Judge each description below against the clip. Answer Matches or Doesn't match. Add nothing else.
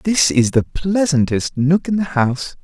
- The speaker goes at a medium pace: Matches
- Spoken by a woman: Doesn't match